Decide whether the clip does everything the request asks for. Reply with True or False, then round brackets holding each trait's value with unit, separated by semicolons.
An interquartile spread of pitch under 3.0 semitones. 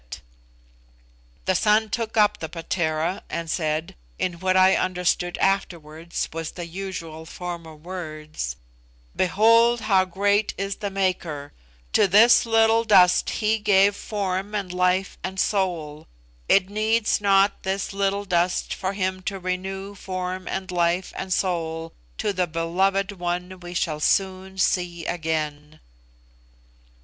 True (2.6 semitones)